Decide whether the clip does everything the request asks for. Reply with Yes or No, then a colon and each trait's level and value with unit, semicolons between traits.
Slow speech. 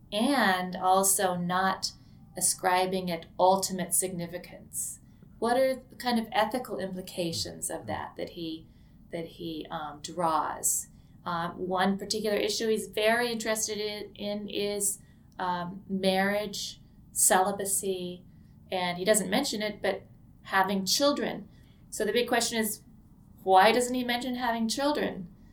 Yes: slow, 125 wpm